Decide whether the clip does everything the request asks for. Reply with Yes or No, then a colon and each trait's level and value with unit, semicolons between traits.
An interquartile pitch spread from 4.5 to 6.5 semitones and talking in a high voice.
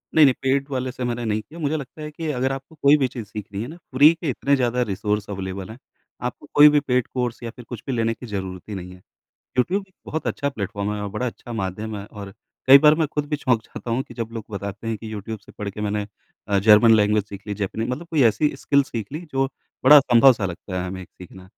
No: average, 4.9 semitones; low, 115 Hz